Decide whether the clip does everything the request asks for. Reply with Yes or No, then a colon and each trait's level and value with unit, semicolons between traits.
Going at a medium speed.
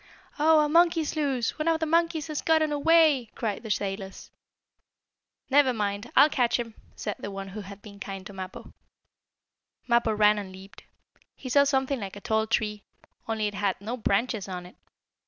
Yes: average, 180 wpm